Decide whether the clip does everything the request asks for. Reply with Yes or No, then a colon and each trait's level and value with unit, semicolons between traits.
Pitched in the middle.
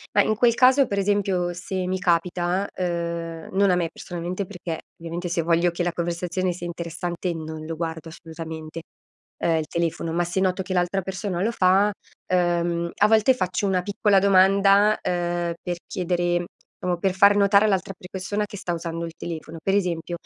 Yes: medium, 180 Hz